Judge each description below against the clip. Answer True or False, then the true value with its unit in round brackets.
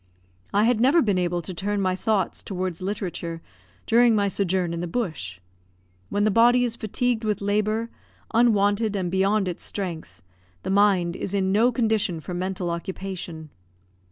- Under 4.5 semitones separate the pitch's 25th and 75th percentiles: True (3.3 semitones)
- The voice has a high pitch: True (195 Hz)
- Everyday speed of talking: True (160 wpm)